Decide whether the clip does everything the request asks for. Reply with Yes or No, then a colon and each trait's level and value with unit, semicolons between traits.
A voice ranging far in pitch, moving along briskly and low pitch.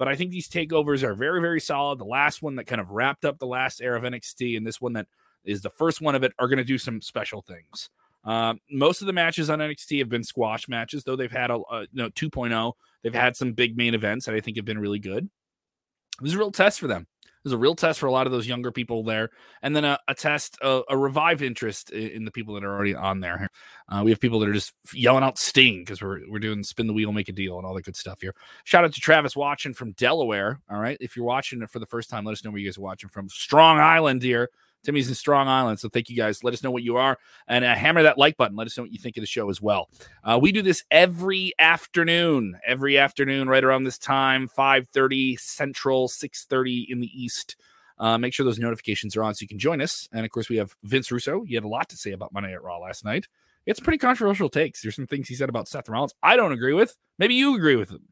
No: average, 4.1 semitones; fast, 270 wpm; low, 125 Hz